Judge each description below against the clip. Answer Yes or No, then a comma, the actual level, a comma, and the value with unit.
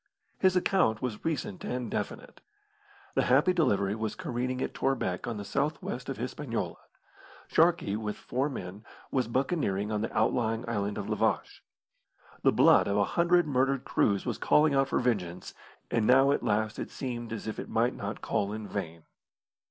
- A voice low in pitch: Yes, low, 120 Hz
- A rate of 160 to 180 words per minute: Yes, average, 175 wpm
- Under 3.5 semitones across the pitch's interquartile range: No, average, 4.7 semitones